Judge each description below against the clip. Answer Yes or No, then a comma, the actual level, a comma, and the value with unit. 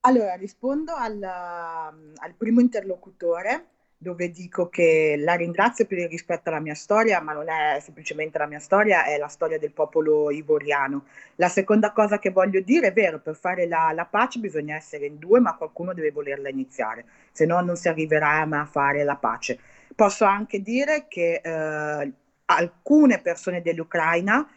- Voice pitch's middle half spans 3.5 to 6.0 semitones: Yes, average, 5.1 semitones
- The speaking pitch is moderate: Yes, medium, 170 Hz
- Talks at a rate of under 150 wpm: No, fast, 170 wpm